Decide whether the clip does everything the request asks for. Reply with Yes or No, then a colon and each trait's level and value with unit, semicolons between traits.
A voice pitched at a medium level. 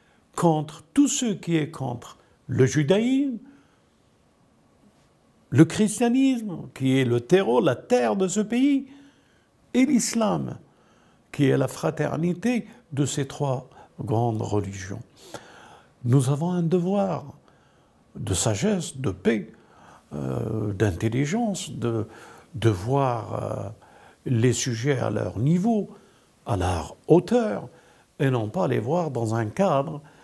Yes: medium, 145 Hz